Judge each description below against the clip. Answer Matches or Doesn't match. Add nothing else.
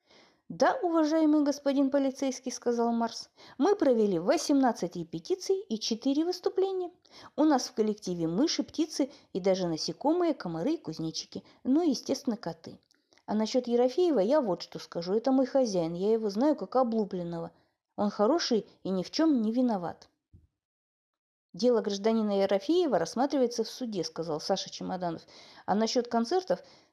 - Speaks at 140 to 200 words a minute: Matches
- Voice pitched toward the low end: Doesn't match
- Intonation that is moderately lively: Doesn't match